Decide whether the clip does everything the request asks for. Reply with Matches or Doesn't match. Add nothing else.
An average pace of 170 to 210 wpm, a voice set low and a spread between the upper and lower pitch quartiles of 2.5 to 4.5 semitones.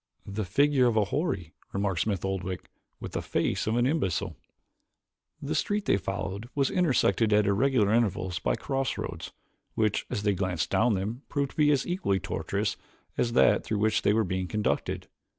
Doesn't match